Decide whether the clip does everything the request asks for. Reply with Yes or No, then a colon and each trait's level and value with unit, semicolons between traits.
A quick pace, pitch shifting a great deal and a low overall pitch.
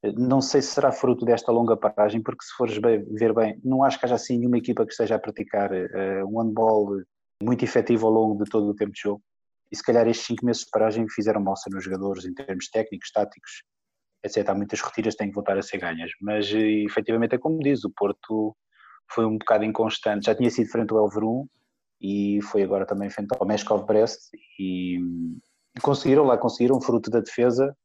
No: fast, 210 wpm; average, 2.8 semitones; low, 110 Hz